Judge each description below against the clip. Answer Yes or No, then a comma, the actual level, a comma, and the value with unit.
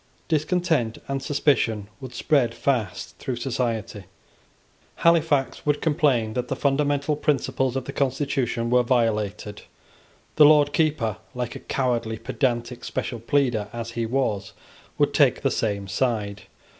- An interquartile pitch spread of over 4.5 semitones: No, average, 4.0 semitones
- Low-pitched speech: Yes, low, 125 Hz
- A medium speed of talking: No, slow, 130 wpm